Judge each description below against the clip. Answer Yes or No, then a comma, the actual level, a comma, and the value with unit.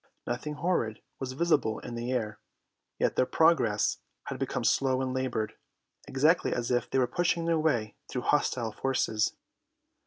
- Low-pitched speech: Yes, low, 130 Hz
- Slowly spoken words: No, average, 155 wpm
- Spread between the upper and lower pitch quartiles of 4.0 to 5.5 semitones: Yes, average, 4.3 semitones